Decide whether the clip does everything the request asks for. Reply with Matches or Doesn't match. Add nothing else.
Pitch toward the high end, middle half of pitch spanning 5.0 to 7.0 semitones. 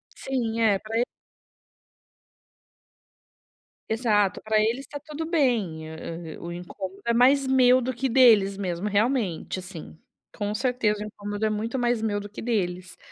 Doesn't match